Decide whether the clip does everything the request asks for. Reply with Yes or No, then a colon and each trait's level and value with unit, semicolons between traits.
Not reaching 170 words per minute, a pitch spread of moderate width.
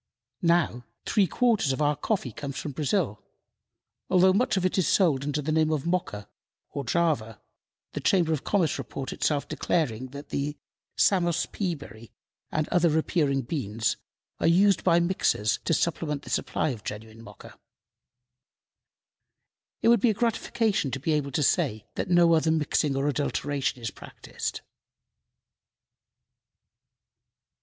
Yes: average, 150 wpm; average, 4.4 semitones